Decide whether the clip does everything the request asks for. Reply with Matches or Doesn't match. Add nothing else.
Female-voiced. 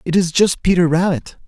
Doesn't match